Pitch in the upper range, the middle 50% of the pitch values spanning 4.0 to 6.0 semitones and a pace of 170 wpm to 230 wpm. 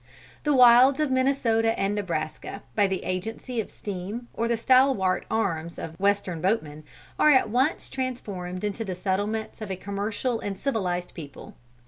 No: high, 205 Hz; average, 4.7 semitones; average, 155 wpm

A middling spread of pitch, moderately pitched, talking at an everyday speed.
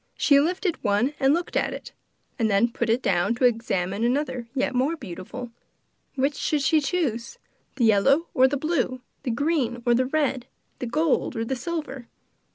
No: average, 4.0 semitones; very high, 255 Hz; average, 180 wpm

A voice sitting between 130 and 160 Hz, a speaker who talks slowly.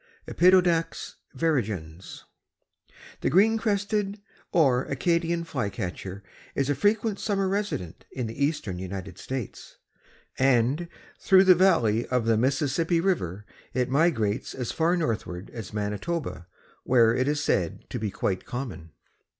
Yes: low, 135 Hz; slow, 125 wpm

